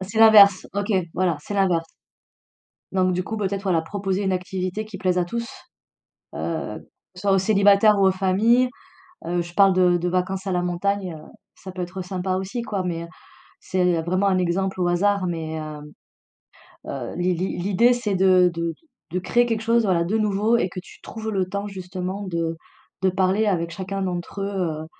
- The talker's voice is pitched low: No, medium, 185 Hz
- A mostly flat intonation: Yes, narrow, 2.1 semitones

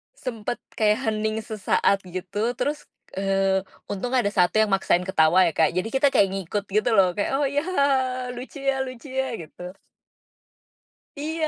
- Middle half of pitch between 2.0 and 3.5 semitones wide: No, average, 5.3 semitones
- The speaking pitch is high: Yes, high, 215 Hz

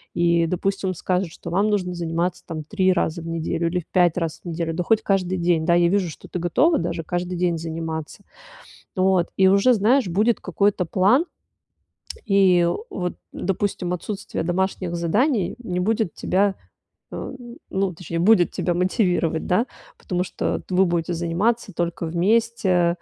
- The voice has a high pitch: No, medium, 180 Hz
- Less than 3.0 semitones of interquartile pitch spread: Yes, narrow, 2.5 semitones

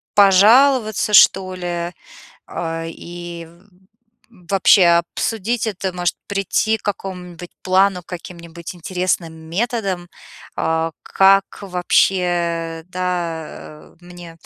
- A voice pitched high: No, medium, 180 Hz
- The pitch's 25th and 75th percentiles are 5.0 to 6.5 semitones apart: No, narrow, 2.4 semitones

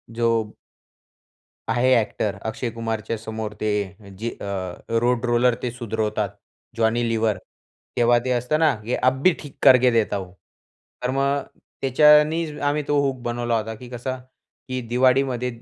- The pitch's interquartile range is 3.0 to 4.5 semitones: No, narrow, 2.6 semitones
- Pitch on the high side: No, low, 120 Hz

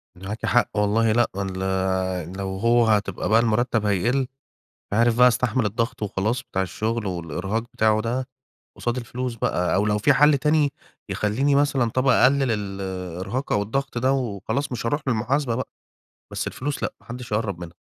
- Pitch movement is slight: No, average, 3.8 semitones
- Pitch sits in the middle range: No, low, 115 Hz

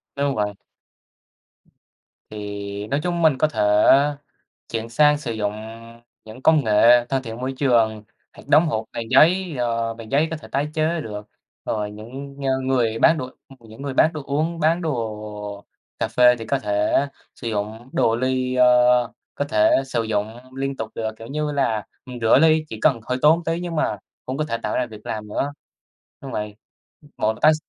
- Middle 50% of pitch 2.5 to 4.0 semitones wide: No, average, 5.0 semitones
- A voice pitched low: Yes, low, 125 Hz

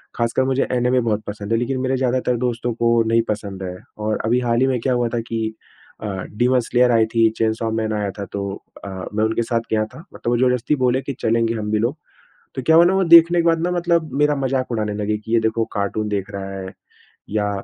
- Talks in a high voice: No, low, 115 Hz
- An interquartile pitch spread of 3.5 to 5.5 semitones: No, average, 3.1 semitones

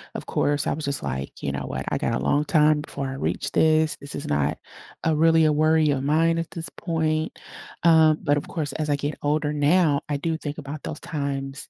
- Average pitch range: No, narrow, 1.9 semitones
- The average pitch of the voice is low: No, medium, 150 Hz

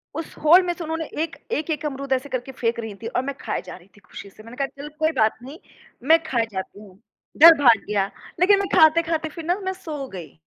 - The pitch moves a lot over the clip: Yes, wide, 6.0 semitones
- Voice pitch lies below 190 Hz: No, very high, 285 Hz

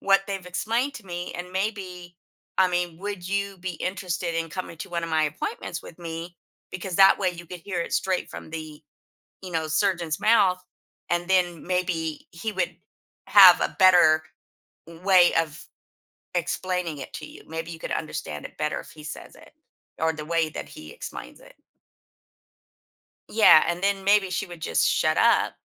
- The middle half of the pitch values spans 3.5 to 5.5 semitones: No, narrow, 2.6 semitones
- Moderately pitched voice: Yes, medium, 175 Hz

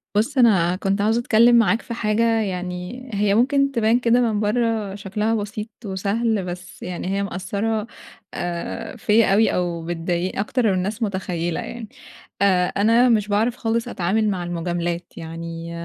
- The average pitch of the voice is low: No, high, 205 Hz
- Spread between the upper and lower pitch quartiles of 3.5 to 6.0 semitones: Yes, average, 4.0 semitones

